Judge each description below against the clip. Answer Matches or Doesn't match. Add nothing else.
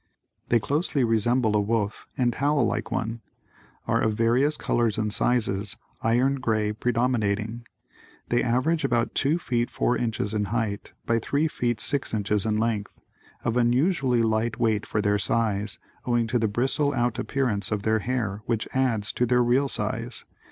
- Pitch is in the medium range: Doesn't match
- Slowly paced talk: Doesn't match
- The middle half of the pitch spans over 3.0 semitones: Doesn't match